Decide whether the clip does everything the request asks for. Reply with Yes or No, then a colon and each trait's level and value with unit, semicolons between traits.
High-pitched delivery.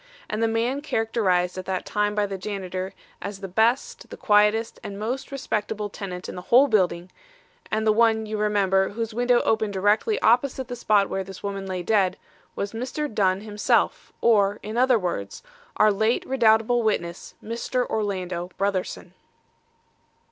Yes: high, 210 Hz